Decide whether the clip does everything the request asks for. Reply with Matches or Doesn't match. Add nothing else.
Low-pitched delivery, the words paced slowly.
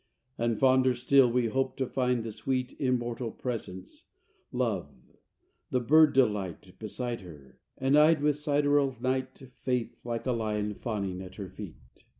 Doesn't match